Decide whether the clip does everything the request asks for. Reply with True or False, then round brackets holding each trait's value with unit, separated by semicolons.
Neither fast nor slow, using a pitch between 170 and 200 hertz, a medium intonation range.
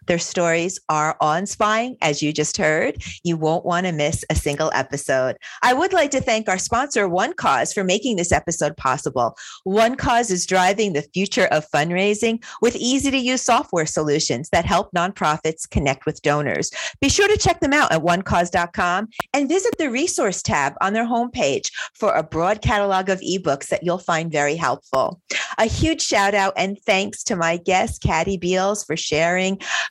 False (185 wpm; 185 Hz; 6.2 semitones)